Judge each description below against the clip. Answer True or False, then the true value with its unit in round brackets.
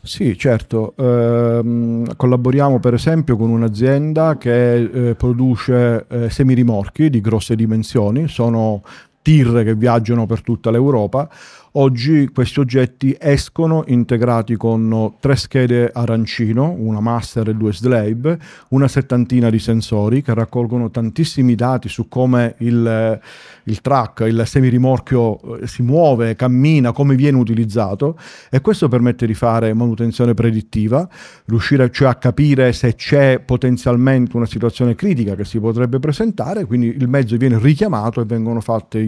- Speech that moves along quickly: False (135 wpm)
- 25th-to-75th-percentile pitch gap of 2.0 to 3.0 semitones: True (2.5 semitones)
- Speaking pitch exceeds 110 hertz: True (120 Hz)